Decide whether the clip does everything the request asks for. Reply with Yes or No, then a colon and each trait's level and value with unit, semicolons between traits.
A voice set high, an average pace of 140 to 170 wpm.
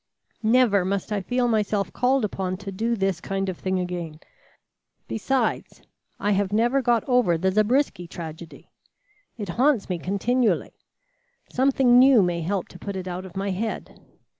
Yes: high, 200 Hz; average, 160 wpm